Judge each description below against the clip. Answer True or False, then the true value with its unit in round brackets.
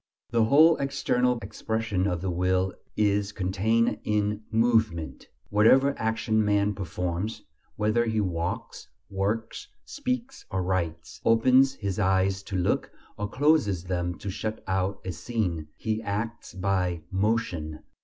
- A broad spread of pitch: False (3.4 semitones)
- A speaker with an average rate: False (130 wpm)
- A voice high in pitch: False (105 Hz)